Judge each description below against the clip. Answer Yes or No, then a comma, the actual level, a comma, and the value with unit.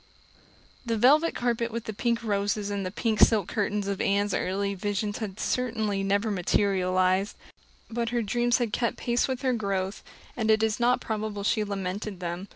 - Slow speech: No, average, 175 wpm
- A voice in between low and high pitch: No, high, 210 Hz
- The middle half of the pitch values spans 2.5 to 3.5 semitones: Yes, average, 2.8 semitones